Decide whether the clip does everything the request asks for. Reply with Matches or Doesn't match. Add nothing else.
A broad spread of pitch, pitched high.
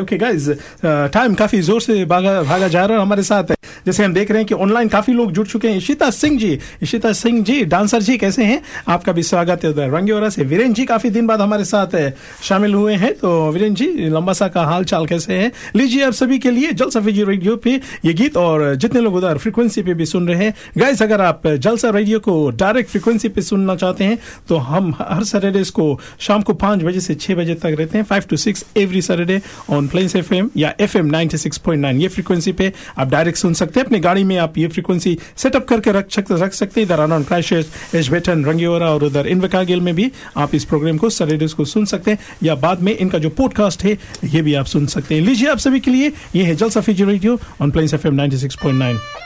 Doesn't match